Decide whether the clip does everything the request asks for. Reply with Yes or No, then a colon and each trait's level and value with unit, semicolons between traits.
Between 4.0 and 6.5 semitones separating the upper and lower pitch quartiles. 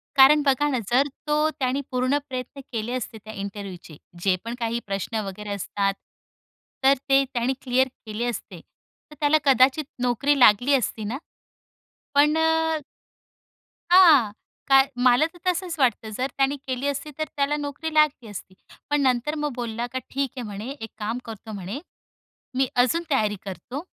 Yes: average, 4.3 semitones